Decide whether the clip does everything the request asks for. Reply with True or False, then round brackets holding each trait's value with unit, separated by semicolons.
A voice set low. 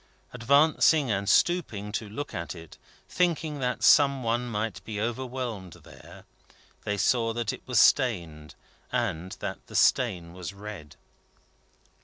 True (115 Hz)